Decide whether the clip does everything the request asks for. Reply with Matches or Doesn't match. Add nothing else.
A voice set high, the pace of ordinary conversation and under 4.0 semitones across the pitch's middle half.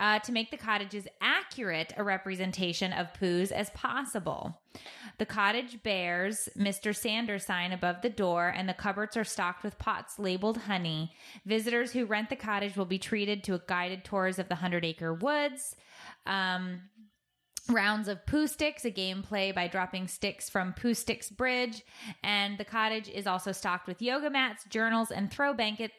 Matches